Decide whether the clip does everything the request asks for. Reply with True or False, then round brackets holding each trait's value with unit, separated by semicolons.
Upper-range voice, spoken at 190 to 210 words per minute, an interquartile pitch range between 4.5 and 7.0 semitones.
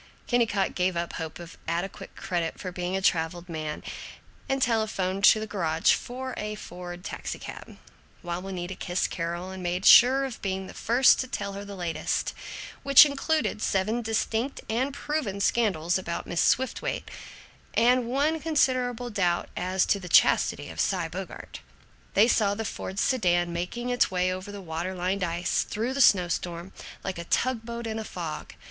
False (195 Hz; 170 wpm; 5.0 semitones)